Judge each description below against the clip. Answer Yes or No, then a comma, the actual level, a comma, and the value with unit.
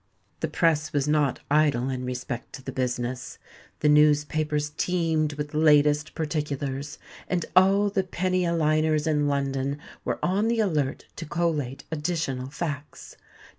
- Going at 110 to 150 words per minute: Yes, average, 140 wpm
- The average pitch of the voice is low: No, medium, 150 Hz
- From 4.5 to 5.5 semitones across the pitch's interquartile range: No, average, 2.7 semitones